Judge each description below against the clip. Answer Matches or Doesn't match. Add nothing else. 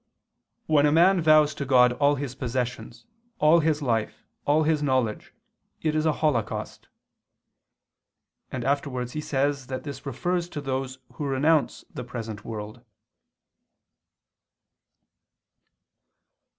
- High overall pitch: Doesn't match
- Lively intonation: Doesn't match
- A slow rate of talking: Matches